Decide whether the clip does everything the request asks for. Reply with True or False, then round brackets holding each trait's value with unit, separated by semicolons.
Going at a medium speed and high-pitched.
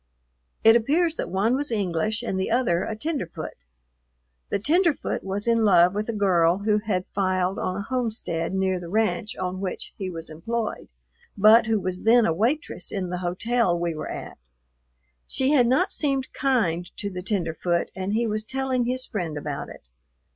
True (180 wpm; 205 Hz)